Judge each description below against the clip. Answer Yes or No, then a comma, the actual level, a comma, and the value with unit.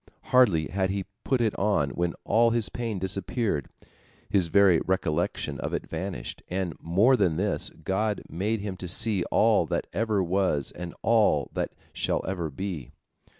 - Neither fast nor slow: Yes, average, 160 wpm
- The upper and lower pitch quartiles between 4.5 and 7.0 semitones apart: No, average, 3.7 semitones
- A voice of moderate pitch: No, very low, 95 Hz